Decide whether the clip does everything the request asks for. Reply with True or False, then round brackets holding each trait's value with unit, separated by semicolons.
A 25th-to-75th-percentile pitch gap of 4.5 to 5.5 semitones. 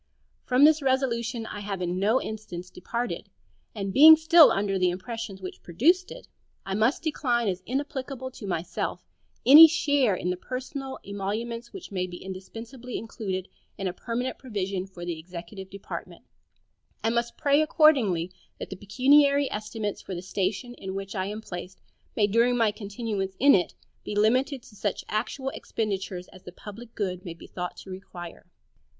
True (5.2 semitones)